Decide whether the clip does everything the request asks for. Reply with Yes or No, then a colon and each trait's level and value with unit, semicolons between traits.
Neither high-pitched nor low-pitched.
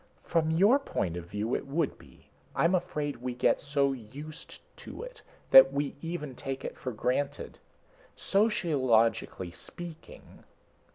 Yes: medium, 145 Hz